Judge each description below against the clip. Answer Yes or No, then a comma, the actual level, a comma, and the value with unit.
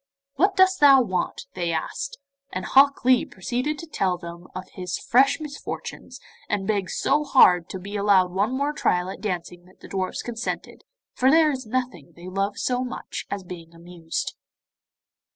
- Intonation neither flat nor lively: No, wide, 6.8 semitones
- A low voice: No, high, 200 Hz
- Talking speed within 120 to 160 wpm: No, average, 170 wpm